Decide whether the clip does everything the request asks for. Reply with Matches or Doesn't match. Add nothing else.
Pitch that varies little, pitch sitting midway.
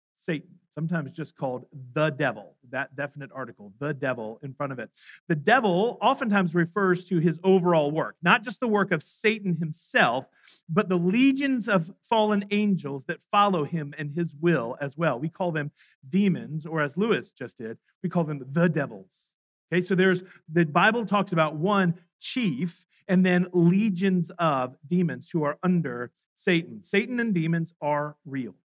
Doesn't match